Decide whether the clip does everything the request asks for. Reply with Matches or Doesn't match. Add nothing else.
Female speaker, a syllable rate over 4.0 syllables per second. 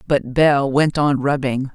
Doesn't match